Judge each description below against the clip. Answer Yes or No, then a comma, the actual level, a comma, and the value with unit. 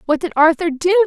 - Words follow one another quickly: Yes, fast, 225 wpm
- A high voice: Yes, very high, 335 Hz